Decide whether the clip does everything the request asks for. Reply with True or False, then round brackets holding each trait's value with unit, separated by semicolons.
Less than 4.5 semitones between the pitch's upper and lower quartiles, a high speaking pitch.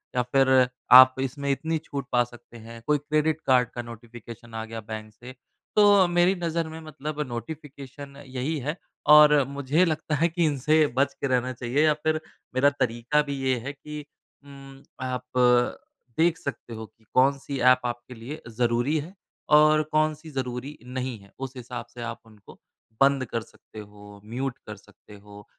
False (3.8 semitones; 135 Hz)